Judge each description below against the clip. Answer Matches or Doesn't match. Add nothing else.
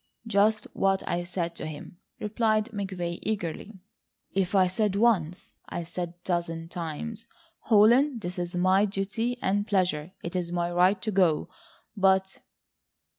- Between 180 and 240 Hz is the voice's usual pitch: Matches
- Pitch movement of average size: Matches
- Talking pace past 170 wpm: Doesn't match